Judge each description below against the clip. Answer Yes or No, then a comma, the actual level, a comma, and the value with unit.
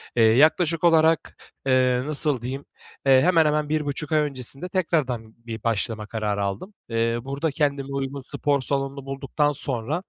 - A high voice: No, medium, 140 Hz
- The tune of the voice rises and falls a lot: No, average, 3.7 semitones